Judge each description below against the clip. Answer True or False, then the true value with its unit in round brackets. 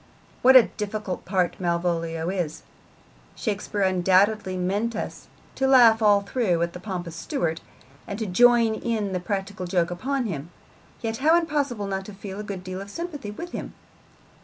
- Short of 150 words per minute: False (170 wpm)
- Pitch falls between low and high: False (200 Hz)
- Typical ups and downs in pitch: True (4.0 semitones)